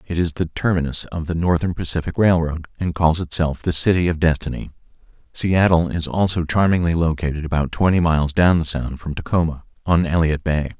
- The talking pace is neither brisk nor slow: Yes, average, 180 wpm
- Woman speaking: No, male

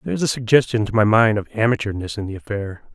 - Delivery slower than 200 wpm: No, fast, 245 wpm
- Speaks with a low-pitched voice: Yes, low, 110 Hz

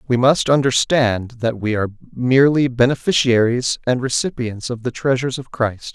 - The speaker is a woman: No, male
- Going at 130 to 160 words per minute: Yes, average, 150 wpm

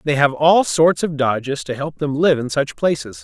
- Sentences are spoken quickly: Yes, fast, 240 wpm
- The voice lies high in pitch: No, medium, 140 Hz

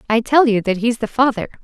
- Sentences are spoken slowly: No, fast, 260 wpm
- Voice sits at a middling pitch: No, high, 230 Hz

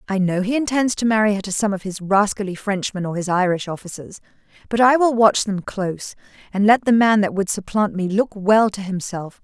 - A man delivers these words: No, female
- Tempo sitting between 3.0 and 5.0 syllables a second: No, 5.5 syllables/s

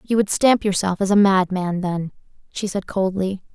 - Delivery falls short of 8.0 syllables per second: Yes, 4.7 syllables/s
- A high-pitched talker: Yes, high, 195 Hz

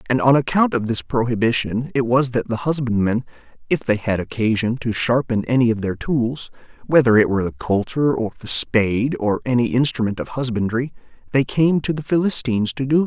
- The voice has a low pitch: Yes, low, 125 Hz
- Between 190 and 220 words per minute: Yes, average, 195 wpm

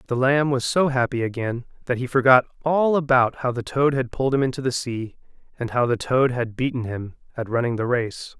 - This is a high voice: No, low, 125 Hz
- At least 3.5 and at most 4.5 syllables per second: No, 5.4 syllables/s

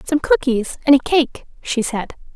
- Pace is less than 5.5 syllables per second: Yes, 4.4 syllables/s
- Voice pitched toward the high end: Yes, very high, 270 Hz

